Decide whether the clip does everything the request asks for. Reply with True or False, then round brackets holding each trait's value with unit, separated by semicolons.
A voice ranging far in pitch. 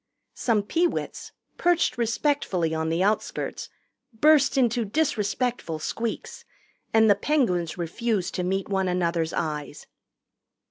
True (6.0 semitones)